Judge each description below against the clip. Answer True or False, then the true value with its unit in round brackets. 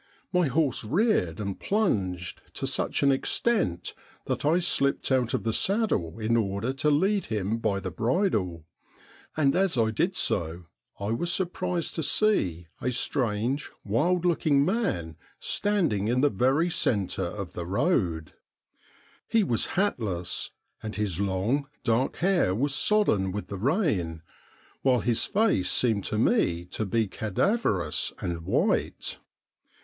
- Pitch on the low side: True (115 Hz)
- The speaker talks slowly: False (145 wpm)